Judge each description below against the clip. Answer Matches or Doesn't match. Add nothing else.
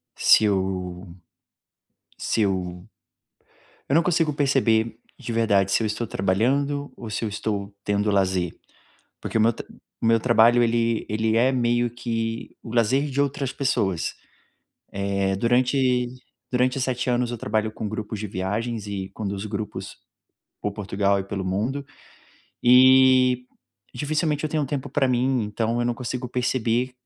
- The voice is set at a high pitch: Doesn't match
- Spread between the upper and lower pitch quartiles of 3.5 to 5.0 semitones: Matches